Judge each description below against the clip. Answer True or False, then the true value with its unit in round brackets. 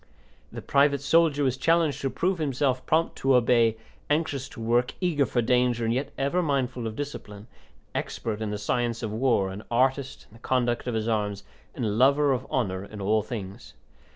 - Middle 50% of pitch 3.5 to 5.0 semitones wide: True (3.9 semitones)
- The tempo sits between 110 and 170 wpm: False (195 wpm)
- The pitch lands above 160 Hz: False (125 Hz)